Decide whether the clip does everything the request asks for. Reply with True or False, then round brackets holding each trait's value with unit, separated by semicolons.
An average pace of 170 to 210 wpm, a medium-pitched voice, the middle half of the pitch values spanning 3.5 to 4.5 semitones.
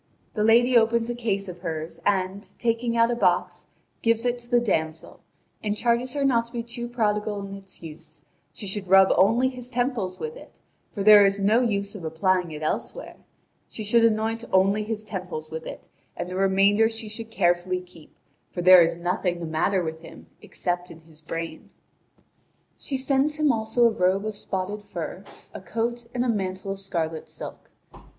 False (190 wpm; 205 Hz; 4.2 semitones)